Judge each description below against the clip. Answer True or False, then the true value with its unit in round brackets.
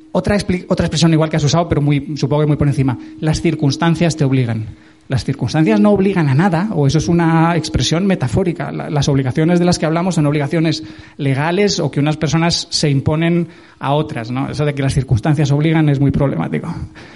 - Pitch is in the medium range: True (155 Hz)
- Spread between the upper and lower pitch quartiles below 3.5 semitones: True (3.0 semitones)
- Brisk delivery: True (205 wpm)